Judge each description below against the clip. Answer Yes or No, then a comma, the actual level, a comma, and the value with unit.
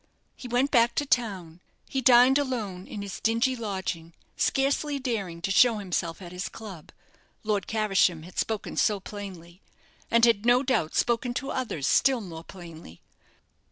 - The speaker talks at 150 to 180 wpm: Yes, average, 155 wpm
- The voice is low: No, high, 215 Hz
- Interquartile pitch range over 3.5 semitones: Yes, average, 5.3 semitones